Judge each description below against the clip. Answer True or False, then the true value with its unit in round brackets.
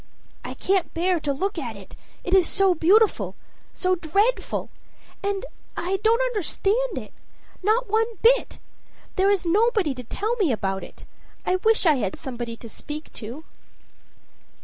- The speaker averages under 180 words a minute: True (150 wpm)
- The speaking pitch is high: True (370 Hz)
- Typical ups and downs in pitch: False (6.4 semitones)